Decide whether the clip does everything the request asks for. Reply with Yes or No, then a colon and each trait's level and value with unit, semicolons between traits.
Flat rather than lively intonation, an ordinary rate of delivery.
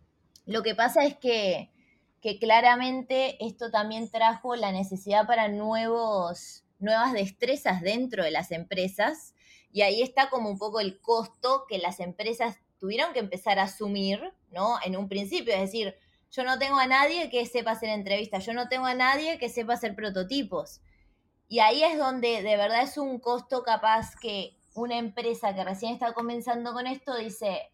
No: average, 3.4 semitones; average, 175 wpm